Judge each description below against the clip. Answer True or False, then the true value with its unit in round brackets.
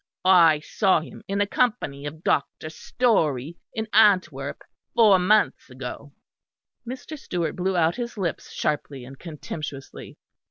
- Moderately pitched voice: True (170 Hz)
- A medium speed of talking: False (130 wpm)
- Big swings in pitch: True (5.8 semitones)